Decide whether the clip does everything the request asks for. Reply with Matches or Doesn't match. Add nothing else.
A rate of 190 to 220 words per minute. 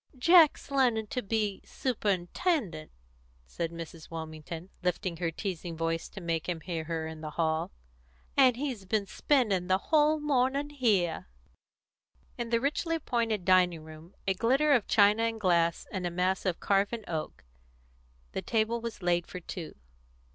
Doesn't match